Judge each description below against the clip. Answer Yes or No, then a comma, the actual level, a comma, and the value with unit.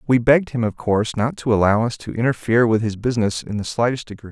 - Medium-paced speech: No, fast, 250 wpm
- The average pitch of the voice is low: Yes, low, 115 Hz